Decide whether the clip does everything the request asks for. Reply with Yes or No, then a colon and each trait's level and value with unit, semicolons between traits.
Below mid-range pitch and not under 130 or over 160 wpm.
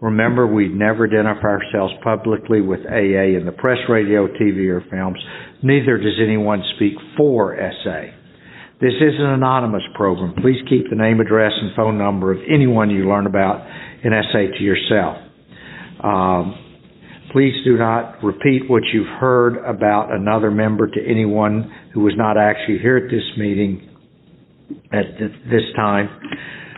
Yes: low, 110 Hz; average, 150 wpm